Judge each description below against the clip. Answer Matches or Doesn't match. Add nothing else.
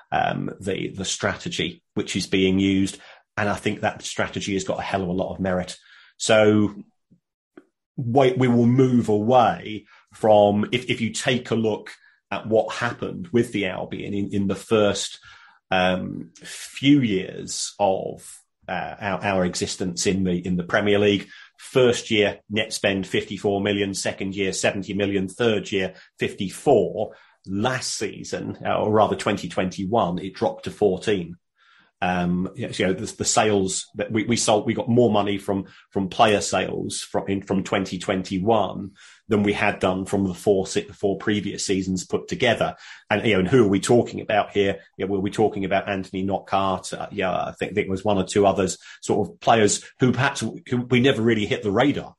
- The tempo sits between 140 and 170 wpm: Doesn't match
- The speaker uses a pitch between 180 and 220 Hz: Doesn't match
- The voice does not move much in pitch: Matches